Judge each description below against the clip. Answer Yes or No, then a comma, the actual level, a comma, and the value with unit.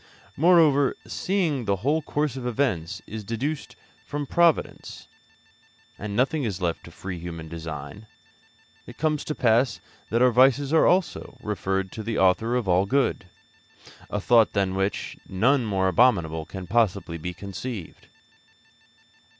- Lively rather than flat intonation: Yes, wide, 6.5 semitones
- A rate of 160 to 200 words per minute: No, average, 145 wpm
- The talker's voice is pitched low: Yes, low, 110 Hz